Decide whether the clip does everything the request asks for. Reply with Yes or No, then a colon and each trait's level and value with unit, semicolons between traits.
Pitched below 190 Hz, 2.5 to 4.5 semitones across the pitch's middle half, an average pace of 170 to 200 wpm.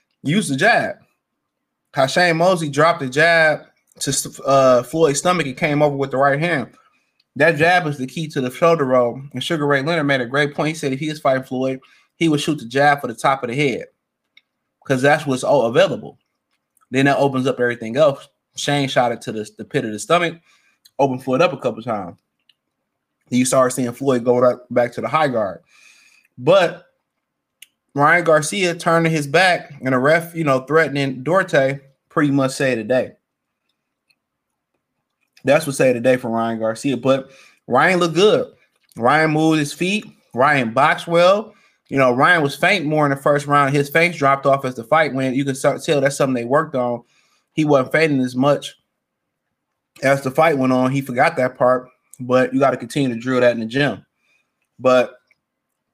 Yes: medium, 140 Hz; average, 3.5 semitones; average, 195 wpm